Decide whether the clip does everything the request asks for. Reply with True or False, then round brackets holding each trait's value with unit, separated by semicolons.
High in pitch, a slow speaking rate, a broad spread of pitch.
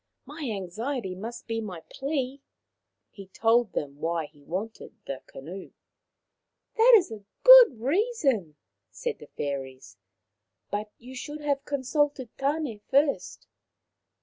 True (230 Hz; 130 wpm; 7.7 semitones)